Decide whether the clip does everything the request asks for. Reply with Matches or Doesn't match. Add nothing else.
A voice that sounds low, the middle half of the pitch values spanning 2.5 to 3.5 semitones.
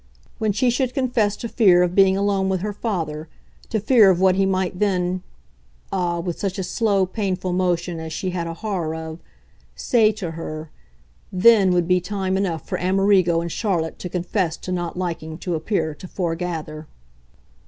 Doesn't match